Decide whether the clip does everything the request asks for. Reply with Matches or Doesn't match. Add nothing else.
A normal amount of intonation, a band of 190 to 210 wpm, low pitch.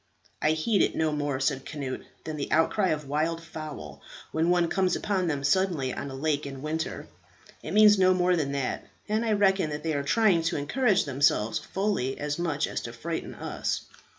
Doesn't match